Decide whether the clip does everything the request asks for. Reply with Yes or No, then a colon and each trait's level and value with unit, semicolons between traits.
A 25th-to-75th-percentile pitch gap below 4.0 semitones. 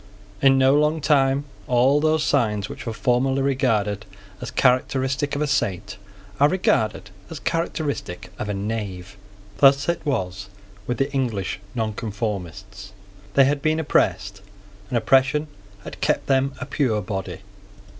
No: average, 5.3 semitones